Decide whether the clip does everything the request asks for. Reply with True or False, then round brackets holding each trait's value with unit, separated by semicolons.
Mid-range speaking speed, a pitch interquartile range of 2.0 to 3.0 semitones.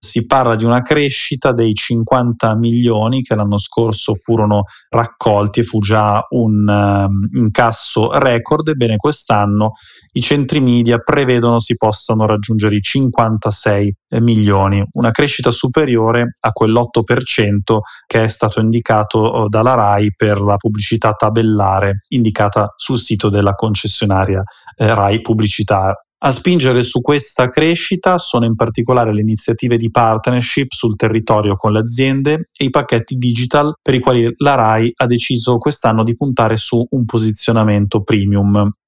True (140 wpm; 2.6 semitones)